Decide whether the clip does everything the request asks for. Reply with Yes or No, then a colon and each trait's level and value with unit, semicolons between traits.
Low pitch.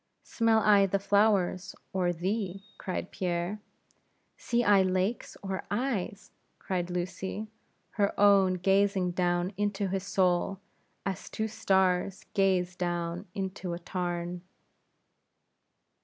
No: high, 190 Hz